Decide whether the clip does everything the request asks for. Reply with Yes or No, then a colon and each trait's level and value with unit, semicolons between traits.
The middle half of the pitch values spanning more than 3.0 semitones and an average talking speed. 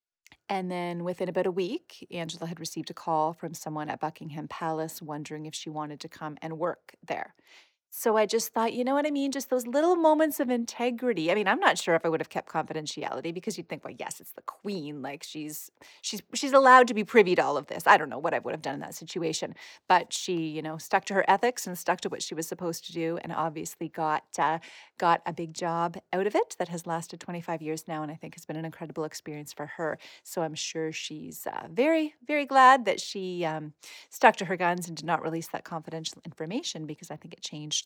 No: average, 3.7 semitones; fast, 245 wpm